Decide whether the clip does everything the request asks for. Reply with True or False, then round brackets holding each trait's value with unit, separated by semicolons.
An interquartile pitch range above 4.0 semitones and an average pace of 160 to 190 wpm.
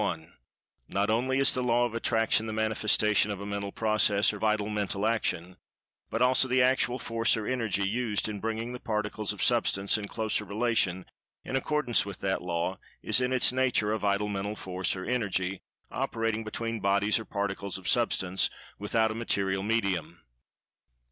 False (2.6 semitones; 170 wpm)